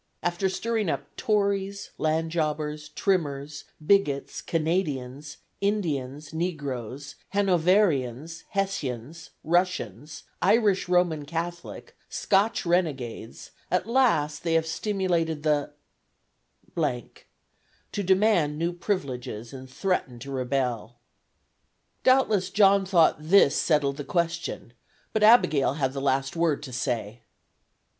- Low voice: No, medium, 160 Hz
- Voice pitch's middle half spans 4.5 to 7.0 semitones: Yes, average, 5.3 semitones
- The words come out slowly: Yes, slow, 105 wpm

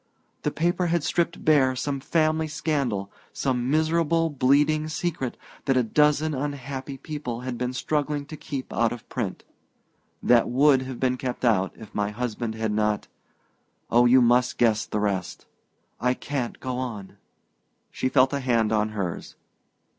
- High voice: No, low, 130 Hz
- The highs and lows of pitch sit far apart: No, average, 4.0 semitones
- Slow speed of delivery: No, average, 155 wpm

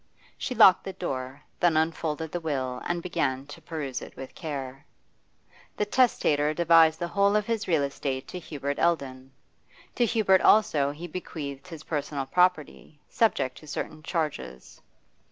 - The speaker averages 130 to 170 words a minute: Yes, average, 155 wpm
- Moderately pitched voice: Yes, medium, 155 Hz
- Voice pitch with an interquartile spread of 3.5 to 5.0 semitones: Yes, average, 4.0 semitones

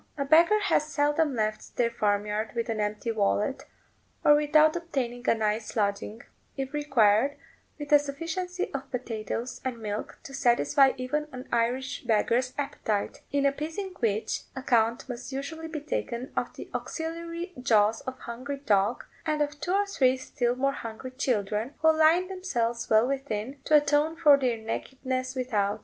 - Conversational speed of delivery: Yes, average, 165 wpm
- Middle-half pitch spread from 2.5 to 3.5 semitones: No, average, 4.6 semitones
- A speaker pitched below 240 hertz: No, very high, 260 Hz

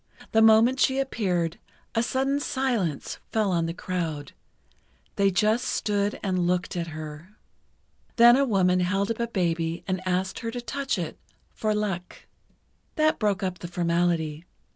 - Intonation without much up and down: No, average, 4.7 semitones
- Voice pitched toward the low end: No, high, 190 Hz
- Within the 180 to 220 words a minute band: No, average, 150 wpm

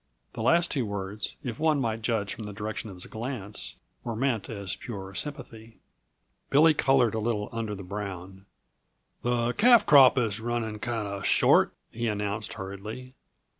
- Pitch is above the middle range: No, low, 110 Hz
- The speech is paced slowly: No, average, 160 wpm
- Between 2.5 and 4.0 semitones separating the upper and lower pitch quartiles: Yes, average, 3.1 semitones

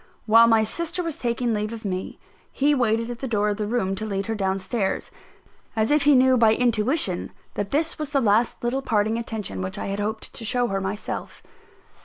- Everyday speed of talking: No, fast, 215 wpm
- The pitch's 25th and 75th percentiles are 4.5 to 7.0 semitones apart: No, average, 3.2 semitones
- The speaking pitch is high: Yes, high, 225 Hz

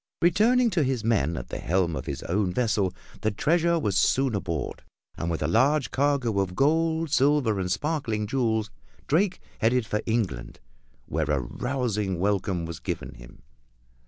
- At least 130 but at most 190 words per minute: Yes, average, 160 wpm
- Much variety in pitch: Yes, wide, 7.5 semitones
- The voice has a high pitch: No, low, 110 Hz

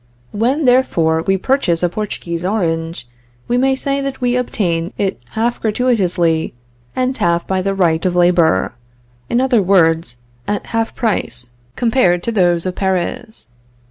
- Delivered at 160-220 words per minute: No, average, 145 wpm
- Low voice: No, high, 190 Hz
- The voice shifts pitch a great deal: Yes, wide, 6.0 semitones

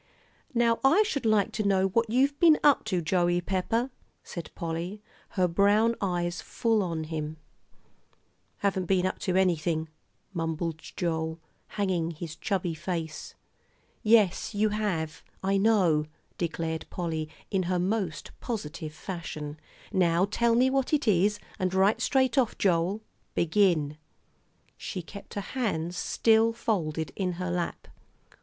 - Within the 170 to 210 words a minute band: No, slow, 135 wpm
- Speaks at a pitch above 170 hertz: Yes, medium, 185 Hz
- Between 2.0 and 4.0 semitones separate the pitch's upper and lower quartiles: No, average, 4.5 semitones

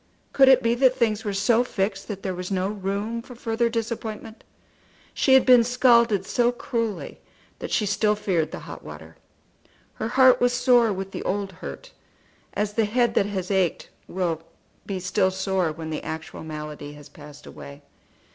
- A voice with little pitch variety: No, average, 4.1 semitones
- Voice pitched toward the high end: Yes, high, 205 Hz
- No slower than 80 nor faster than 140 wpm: No, average, 175 wpm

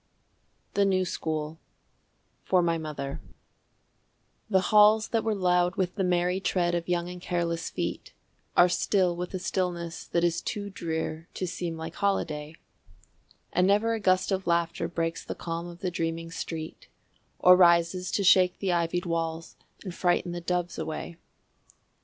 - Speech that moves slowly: No, average, 160 wpm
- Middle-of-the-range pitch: Yes, medium, 175 Hz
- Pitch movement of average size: No, narrow, 1.8 semitones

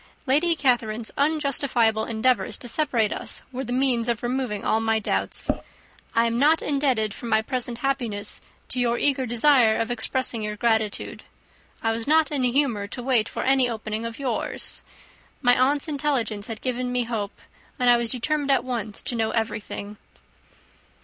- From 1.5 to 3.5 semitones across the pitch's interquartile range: Yes, average, 3.2 semitones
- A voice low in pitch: No, high, 240 Hz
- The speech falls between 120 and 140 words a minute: No, average, 170 wpm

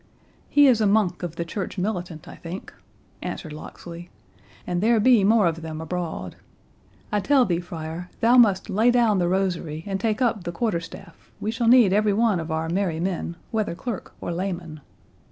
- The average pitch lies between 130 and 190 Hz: Yes, medium, 185 Hz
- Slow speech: No, average, 190 wpm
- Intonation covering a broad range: No, average, 4.3 semitones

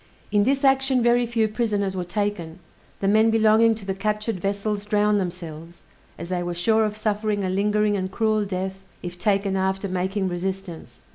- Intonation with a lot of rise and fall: No, narrow, 2.5 semitones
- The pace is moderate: Yes, average, 180 wpm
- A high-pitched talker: Yes, high, 205 Hz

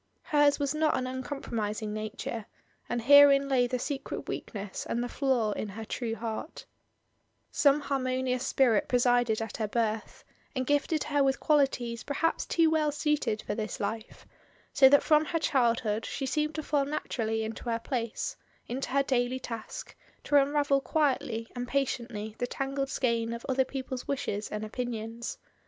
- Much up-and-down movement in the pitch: No, average, 3.6 semitones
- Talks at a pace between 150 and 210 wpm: Yes, average, 165 wpm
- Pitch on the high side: Yes, very high, 255 Hz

